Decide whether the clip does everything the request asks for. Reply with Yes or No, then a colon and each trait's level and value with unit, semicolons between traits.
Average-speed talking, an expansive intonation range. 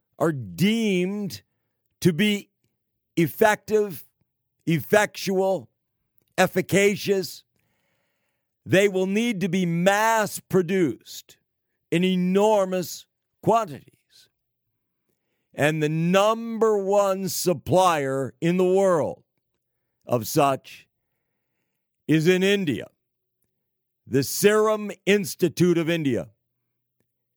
No: slow, 75 wpm; wide, 6.3 semitones